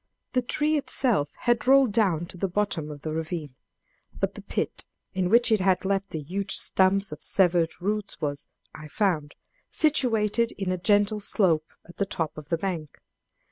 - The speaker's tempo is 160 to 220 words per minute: Yes, average, 180 wpm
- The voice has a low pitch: No, high, 190 Hz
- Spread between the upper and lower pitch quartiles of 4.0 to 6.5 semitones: Yes, average, 4.5 semitones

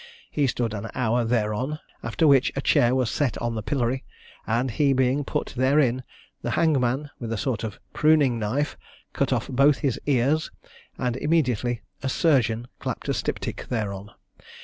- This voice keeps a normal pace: Yes, average, 165 wpm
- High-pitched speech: No, low, 125 Hz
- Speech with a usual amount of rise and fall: Yes, average, 3.4 semitones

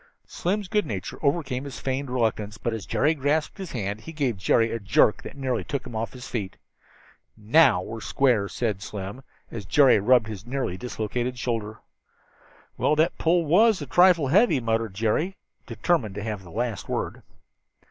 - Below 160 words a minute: No, average, 175 wpm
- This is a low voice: Yes, low, 125 Hz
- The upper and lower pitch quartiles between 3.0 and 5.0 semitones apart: No, wide, 5.4 semitones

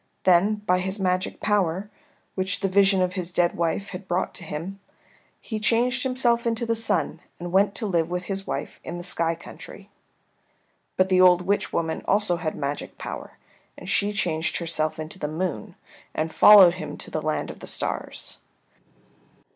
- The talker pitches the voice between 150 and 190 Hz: Yes, medium, 185 Hz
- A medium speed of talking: Yes, average, 180 wpm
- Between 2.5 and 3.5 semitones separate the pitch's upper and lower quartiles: Yes, average, 3.1 semitones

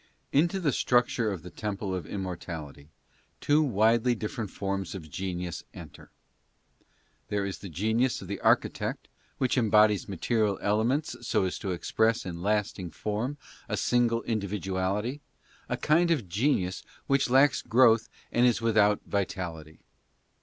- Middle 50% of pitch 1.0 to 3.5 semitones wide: No, average, 4.3 semitones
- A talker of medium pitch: No, low, 105 Hz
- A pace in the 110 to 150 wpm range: Yes, average, 140 wpm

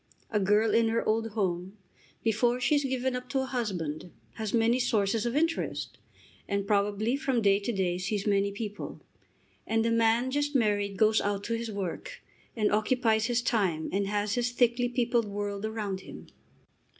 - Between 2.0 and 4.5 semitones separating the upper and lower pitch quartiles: Yes, average, 3.1 semitones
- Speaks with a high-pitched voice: Yes, high, 220 Hz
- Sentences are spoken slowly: No, average, 175 wpm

